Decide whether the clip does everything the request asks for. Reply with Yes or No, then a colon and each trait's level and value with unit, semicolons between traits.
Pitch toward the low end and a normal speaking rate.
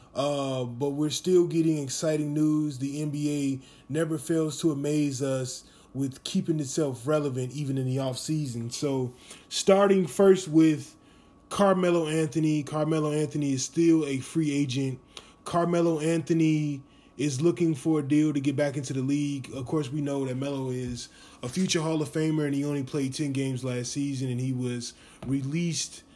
No: medium, 145 Hz; average, 165 wpm